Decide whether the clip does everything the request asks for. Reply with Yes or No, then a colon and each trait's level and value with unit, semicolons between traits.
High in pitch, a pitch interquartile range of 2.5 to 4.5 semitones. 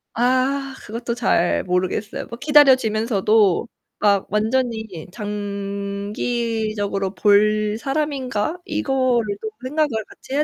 Yes: high, 220 Hz; average, 4.0 semitones